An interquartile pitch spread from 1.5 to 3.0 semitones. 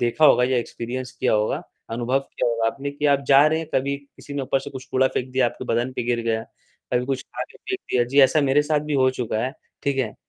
Yes: average, 2.7 semitones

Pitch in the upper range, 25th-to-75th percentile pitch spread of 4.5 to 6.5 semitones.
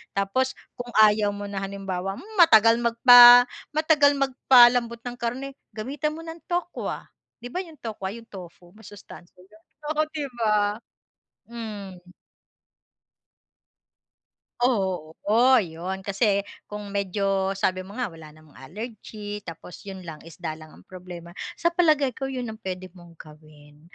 Yes: high, 210 Hz; average, 5.0 semitones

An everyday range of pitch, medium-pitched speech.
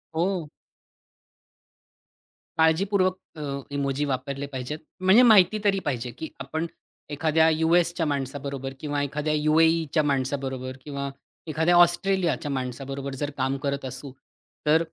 Yes: average, 3.1 semitones; medium, 150 Hz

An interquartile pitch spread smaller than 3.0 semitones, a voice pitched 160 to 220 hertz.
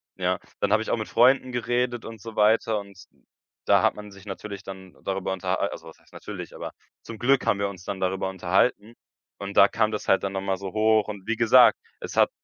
No: narrow, 2.6 semitones; low, 100 Hz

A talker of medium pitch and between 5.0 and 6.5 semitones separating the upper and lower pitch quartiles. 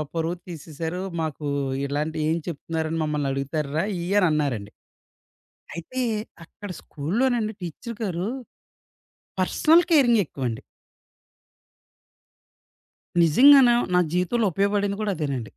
Yes: medium, 170 Hz; wide, 5.4 semitones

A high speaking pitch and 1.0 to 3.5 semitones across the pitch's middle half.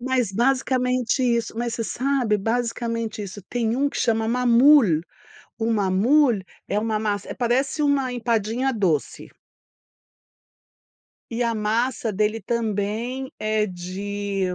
Yes: high, 230 Hz; average, 3.0 semitones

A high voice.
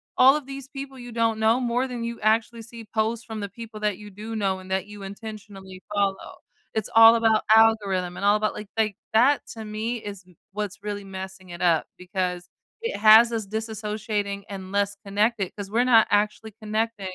Yes: high, 215 Hz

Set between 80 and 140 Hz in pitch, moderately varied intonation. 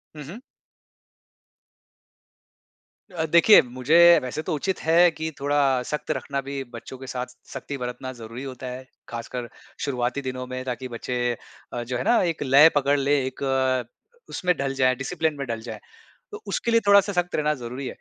Yes: low, 135 Hz; average, 3.8 semitones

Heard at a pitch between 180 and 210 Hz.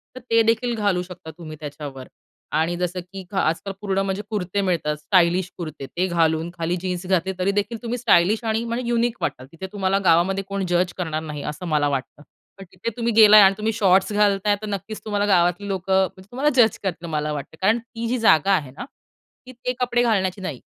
Yes: high, 190 Hz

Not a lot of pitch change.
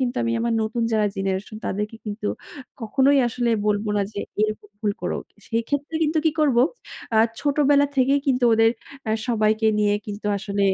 No: average, 4.1 semitones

